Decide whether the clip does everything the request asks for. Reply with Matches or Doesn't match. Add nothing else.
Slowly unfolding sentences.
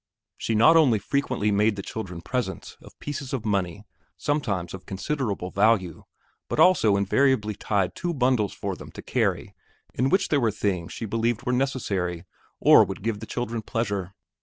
Doesn't match